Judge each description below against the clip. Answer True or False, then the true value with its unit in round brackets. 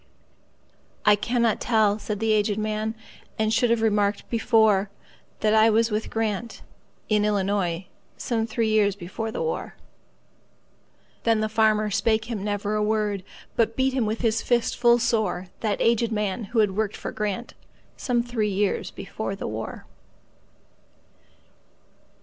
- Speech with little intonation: True (1.6 semitones)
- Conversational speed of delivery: False (125 wpm)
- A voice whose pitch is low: False (215 Hz)